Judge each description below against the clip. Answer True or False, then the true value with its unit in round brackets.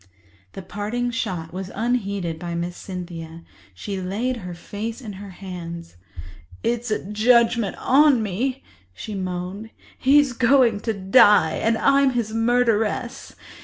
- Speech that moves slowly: True (130 wpm)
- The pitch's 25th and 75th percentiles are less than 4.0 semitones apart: False (4.8 semitones)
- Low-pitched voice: False (210 Hz)